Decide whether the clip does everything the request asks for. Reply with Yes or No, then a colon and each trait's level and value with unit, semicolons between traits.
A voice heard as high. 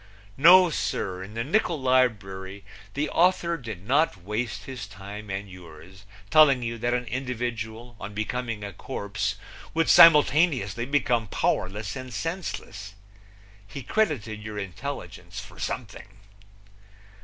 No: low, 115 Hz